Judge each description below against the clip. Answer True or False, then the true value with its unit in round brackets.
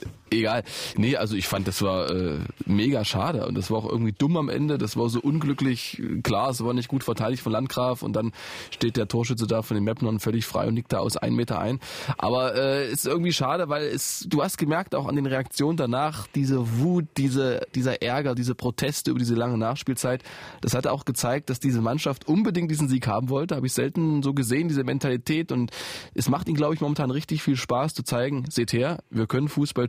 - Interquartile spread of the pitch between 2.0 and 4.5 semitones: True (3.4 semitones)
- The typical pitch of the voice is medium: False (130 Hz)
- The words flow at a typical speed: False (225 wpm)